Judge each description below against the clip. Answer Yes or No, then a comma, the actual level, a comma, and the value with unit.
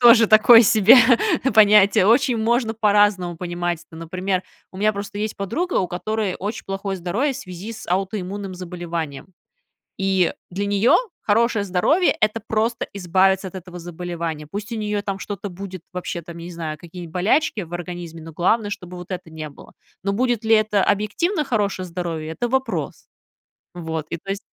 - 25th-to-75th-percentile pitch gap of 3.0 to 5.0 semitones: Yes, average, 3.5 semitones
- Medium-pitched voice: No, high, 195 Hz